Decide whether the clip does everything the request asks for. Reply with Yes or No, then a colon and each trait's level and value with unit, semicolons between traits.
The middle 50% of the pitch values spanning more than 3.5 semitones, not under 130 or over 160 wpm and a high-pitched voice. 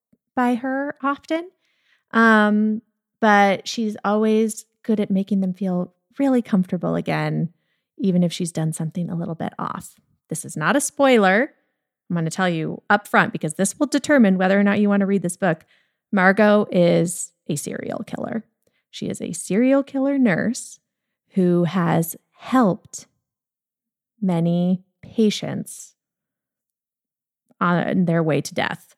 Yes: average, 4.7 semitones; average, 145 wpm; high, 205 Hz